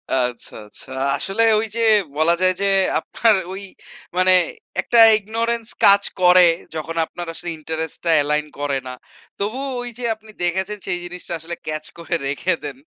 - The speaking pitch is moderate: Yes, medium, 180 Hz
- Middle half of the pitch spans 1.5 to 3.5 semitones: No, average, 4.9 semitones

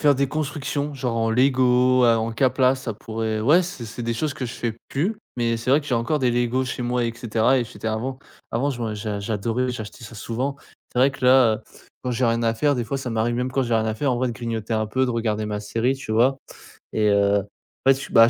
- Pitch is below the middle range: Yes, low, 120 Hz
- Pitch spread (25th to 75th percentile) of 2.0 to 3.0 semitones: Yes, average, 2.7 semitones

